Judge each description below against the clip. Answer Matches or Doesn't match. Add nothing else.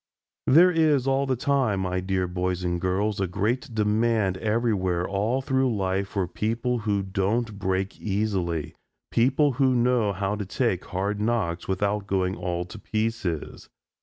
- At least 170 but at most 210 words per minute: Doesn't match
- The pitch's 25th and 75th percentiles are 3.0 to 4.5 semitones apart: Matches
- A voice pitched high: Doesn't match